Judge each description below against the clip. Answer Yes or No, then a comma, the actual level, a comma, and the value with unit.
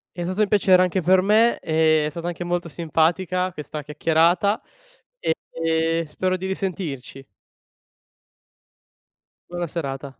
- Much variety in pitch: No, average, 2.7 semitones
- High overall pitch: No, medium, 170 Hz